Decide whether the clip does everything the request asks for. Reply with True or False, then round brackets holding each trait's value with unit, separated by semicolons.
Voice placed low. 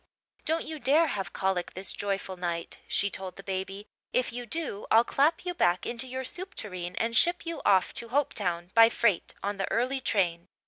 False (210 Hz)